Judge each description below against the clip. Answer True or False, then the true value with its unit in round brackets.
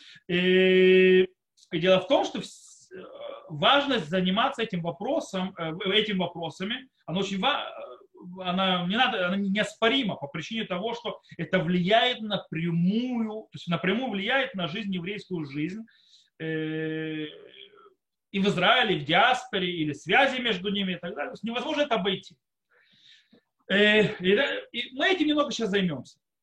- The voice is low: False (195 Hz)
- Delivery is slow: False (125 wpm)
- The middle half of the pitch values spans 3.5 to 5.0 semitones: True (4.6 semitones)